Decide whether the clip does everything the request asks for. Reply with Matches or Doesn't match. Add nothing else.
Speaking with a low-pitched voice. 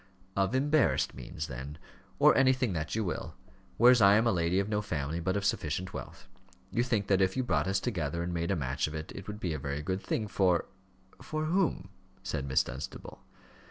Matches